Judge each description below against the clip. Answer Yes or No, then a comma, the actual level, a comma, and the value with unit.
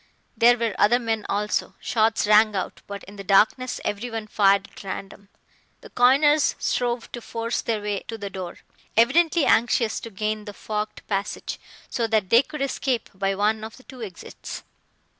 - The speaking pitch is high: Yes, high, 220 Hz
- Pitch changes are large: No, average, 2.8 semitones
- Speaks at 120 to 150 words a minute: No, average, 175 wpm